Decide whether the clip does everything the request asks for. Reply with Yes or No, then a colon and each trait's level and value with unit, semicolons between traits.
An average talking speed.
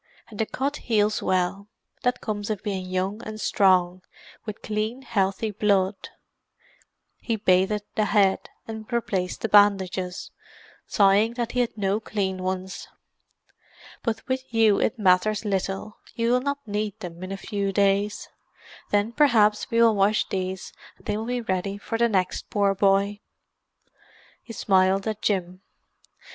Yes: average, 150 wpm